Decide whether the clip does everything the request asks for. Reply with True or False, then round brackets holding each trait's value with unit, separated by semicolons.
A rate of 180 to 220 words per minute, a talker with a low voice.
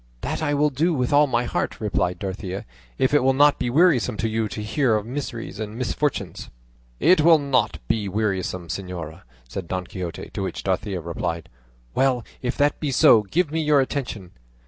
True (190 wpm; 120 Hz)